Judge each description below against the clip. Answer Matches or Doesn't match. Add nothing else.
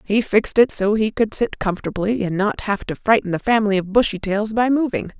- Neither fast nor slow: Doesn't match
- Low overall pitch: Doesn't match